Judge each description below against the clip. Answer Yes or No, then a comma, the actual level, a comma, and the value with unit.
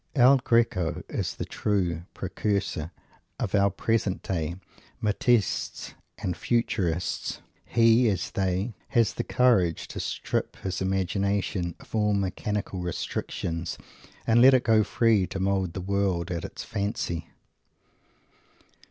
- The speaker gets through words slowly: Yes, slow, 125 wpm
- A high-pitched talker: No, low, 100 Hz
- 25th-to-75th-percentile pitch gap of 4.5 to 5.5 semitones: No, average, 4.0 semitones